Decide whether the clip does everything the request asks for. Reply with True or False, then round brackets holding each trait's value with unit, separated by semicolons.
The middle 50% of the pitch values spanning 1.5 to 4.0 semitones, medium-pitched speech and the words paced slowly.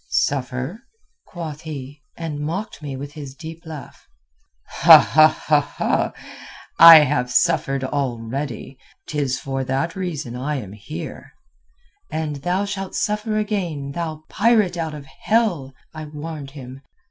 True (3.6 semitones; 150 Hz; 120 wpm)